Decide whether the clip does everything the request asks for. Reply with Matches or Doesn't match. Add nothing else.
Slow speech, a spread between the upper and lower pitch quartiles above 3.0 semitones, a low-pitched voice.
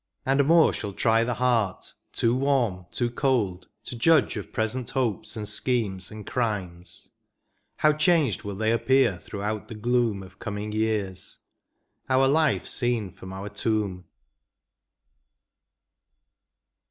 Matches